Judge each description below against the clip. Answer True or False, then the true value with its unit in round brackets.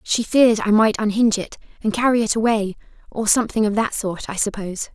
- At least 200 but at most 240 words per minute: True (205 wpm)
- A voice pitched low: False (215 Hz)